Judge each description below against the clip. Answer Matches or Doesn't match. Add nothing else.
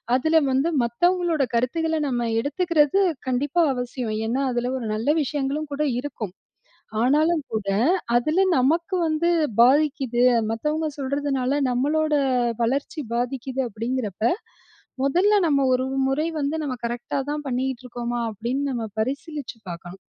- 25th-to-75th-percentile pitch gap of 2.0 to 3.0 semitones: Doesn't match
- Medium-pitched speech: Doesn't match